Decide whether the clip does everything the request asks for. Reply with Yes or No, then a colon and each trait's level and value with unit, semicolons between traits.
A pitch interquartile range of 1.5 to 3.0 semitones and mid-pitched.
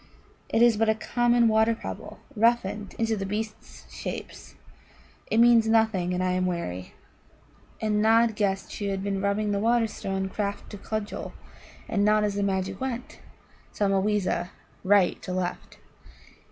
No: narrow, 2.5 semitones; high, 210 Hz